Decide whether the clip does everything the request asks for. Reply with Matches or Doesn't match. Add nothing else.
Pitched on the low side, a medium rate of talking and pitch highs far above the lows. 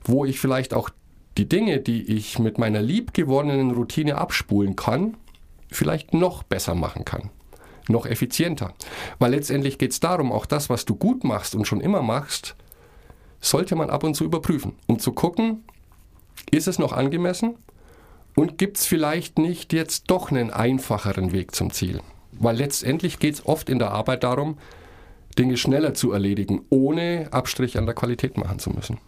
Matches